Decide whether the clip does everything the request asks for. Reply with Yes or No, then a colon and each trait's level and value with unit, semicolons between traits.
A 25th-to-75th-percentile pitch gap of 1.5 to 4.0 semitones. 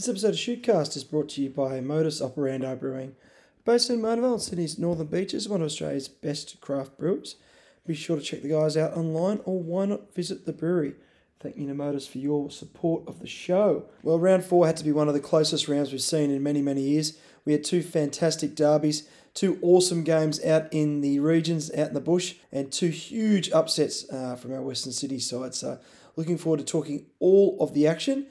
Yes: average, 3.4 semitones